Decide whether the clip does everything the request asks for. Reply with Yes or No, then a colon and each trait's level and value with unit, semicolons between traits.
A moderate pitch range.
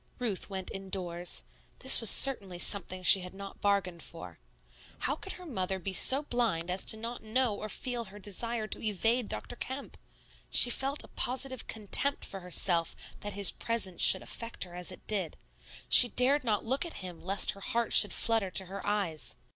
Yes: average, 4.3 semitones